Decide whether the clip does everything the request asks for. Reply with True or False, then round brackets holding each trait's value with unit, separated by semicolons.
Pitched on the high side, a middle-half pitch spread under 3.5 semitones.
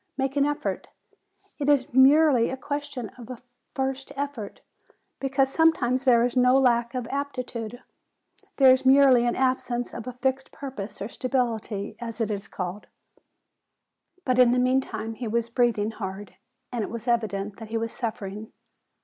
True (245 Hz; 2.9 semitones)